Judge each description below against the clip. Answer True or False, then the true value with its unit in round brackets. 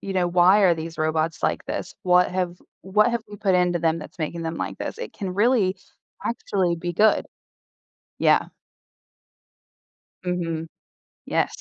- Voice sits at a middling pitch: True (180 Hz)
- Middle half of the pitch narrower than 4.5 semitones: True (2.8 semitones)